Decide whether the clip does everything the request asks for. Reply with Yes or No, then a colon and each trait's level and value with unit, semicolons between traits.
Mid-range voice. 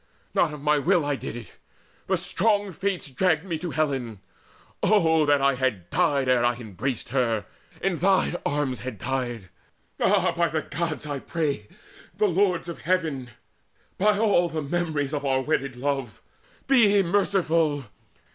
Yes: medium, 150 Hz